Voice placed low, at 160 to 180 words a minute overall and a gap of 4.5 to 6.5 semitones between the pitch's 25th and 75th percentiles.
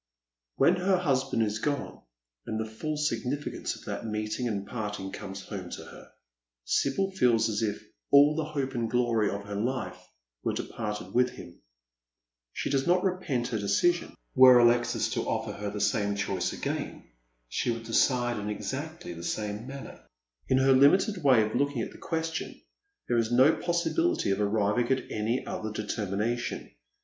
Yes: low, 120 Hz; average, 170 wpm; average, 5.0 semitones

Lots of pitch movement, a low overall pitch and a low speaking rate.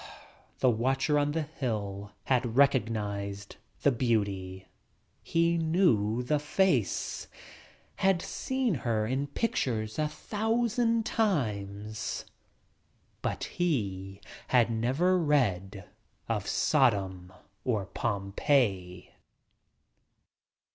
Yes: wide, 7.1 semitones; low, 120 Hz; slow, 90 wpm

